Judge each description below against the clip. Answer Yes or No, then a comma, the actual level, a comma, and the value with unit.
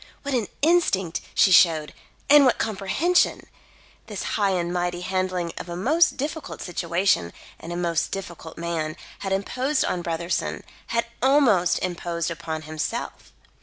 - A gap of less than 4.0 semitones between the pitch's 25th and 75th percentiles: No, wide, 5.5 semitones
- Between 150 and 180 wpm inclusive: No, average, 140 wpm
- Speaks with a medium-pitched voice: Yes, medium, 180 Hz